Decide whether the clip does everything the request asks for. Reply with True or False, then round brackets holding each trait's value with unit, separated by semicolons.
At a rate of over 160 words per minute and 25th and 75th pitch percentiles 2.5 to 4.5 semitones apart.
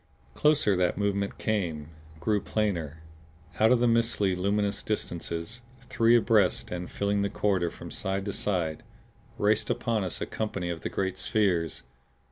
False (150 wpm; 3.4 semitones)